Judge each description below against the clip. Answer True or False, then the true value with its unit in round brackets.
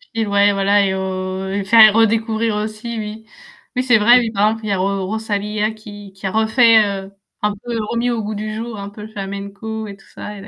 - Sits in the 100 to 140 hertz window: False (210 Hz)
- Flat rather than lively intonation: True (1.8 semitones)